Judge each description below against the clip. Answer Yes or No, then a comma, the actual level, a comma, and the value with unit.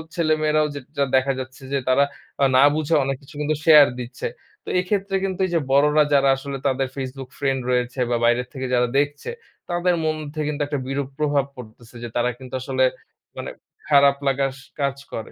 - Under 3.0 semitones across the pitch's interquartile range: Yes, narrow, 2.6 semitones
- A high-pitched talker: No, medium, 140 Hz